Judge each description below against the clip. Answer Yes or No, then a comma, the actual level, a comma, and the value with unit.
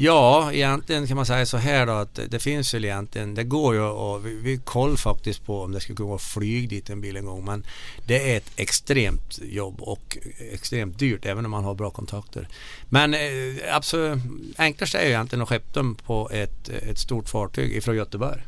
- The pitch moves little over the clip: No, average, 4.3 semitones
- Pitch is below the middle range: Yes, low, 115 Hz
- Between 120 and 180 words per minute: No, fast, 205 wpm